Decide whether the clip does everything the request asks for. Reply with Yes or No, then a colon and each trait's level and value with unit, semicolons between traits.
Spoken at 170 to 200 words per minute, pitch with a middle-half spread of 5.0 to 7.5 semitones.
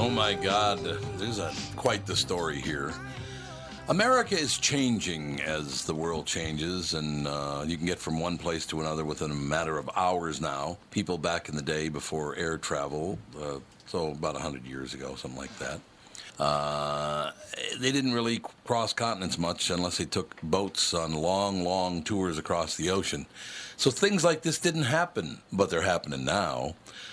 Yes: average, 175 wpm; average, 5.3 semitones